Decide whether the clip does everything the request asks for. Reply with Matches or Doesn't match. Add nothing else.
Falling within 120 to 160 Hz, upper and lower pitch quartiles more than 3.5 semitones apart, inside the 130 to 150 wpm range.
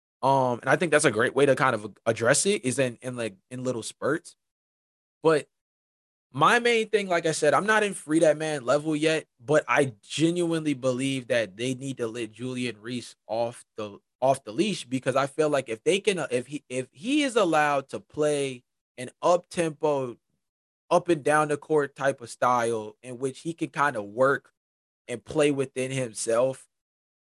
Doesn't match